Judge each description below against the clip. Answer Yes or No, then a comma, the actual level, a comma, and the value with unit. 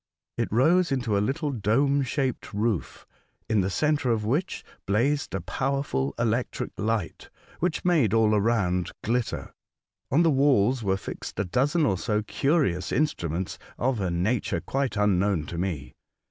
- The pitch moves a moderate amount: No, wide, 5.9 semitones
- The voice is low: Yes, low, 115 Hz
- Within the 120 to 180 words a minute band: Yes, average, 150 wpm